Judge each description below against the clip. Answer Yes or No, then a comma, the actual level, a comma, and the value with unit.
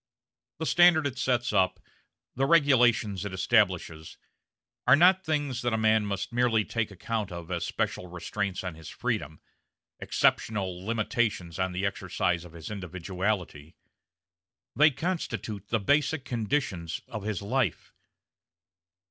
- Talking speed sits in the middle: No, slow, 130 wpm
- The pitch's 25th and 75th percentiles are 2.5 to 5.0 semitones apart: No, wide, 5.5 semitones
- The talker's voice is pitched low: Yes, low, 105 Hz